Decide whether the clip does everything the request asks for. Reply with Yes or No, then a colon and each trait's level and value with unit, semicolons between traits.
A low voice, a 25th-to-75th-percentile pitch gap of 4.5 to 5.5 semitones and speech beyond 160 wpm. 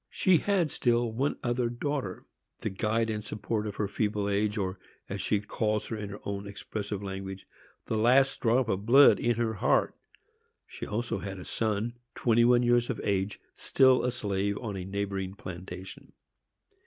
No: low, 105 Hz; average, 3.2 semitones; average, 175 wpm